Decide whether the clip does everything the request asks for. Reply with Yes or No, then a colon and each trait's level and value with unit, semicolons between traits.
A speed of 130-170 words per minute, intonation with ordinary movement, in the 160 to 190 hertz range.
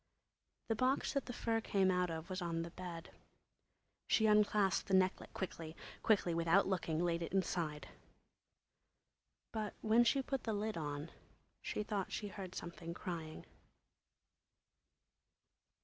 Yes: slow, 135 wpm; average, 4.1 semitones; medium, 185 Hz